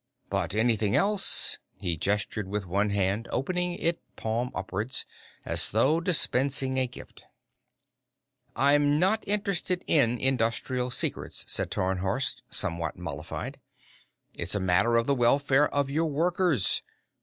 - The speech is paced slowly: Yes, slow, 130 wpm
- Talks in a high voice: No, low, 125 Hz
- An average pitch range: No, wide, 6.3 semitones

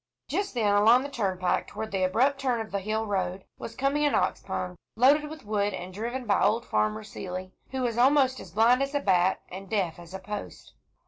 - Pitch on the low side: No, high, 215 Hz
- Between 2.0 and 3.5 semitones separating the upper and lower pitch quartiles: No, wide, 5.5 semitones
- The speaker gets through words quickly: Yes, fast, 215 wpm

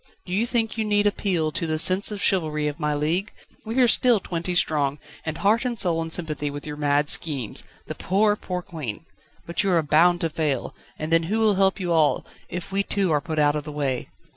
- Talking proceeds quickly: Yes, fast, 230 wpm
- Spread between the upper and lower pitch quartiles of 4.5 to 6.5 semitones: Yes, average, 4.8 semitones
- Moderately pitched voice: Yes, medium, 165 Hz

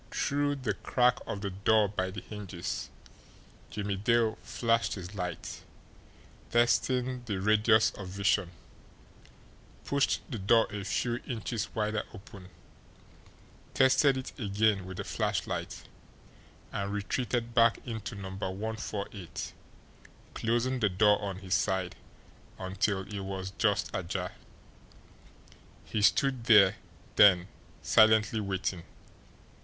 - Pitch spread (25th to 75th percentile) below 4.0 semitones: Yes, average, 3.1 semitones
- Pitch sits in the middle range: No, low, 105 Hz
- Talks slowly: Yes, slow, 115 wpm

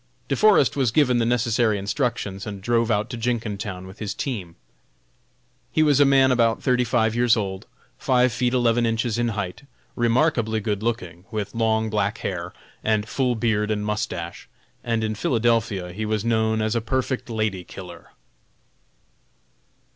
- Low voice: Yes, low, 110 Hz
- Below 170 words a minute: Yes, average, 160 wpm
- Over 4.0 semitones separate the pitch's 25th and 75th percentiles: No, narrow, 2.6 semitones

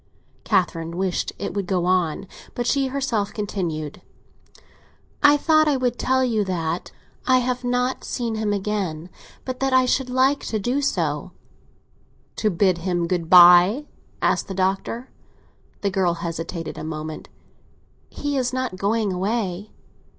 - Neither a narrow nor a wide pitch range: No, wide, 6.1 semitones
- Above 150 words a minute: No, average, 145 wpm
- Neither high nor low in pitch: No, high, 200 Hz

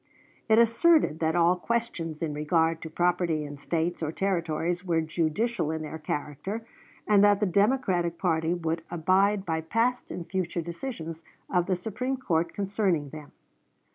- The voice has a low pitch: No, medium, 175 Hz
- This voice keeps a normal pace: Yes, average, 155 wpm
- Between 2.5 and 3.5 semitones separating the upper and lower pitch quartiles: No, average, 4.0 semitones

